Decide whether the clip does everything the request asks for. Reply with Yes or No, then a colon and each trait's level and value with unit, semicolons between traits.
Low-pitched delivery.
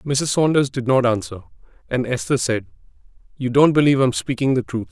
Yes: low, 130 Hz